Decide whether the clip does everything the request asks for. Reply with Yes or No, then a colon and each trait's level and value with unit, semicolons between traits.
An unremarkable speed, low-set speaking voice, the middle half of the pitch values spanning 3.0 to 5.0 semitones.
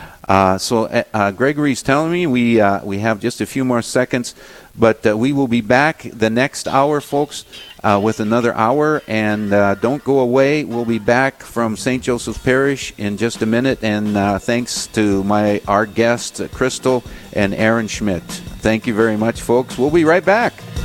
Yes: average, 185 wpm; low, 115 Hz; average, 3.7 semitones